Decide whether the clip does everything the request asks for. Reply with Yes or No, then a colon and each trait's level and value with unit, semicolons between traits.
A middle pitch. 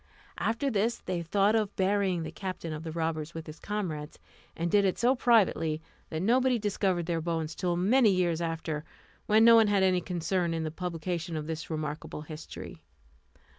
Yes: medium, 175 Hz